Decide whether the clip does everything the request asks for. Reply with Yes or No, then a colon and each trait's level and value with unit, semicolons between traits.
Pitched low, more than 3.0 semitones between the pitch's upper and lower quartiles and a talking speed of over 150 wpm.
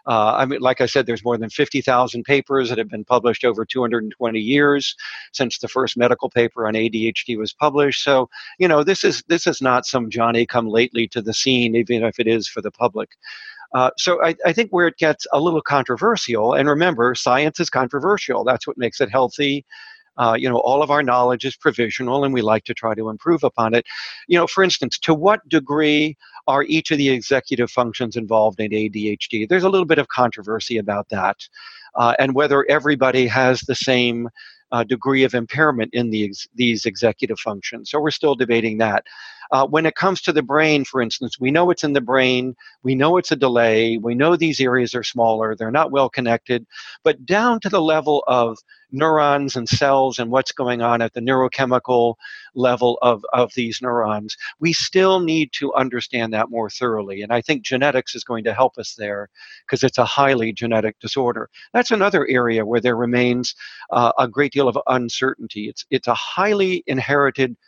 Yes: low, 125 Hz; average, 3.8 semitones; fast, 205 wpm